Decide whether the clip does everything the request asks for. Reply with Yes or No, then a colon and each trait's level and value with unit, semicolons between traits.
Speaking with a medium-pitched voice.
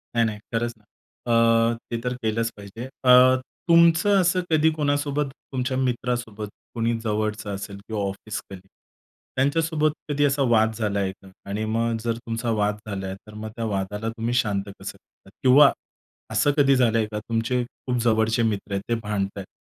No: low, 115 Hz